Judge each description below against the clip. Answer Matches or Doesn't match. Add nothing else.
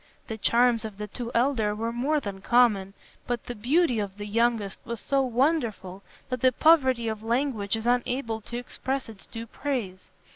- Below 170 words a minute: Doesn't match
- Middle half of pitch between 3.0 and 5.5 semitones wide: Matches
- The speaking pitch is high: Matches